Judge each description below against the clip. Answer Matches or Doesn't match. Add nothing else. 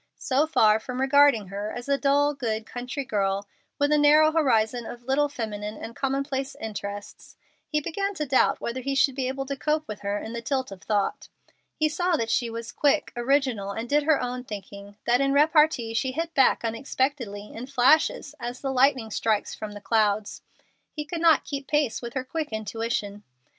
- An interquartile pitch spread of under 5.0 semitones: Matches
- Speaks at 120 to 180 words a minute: Doesn't match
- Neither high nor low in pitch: Doesn't match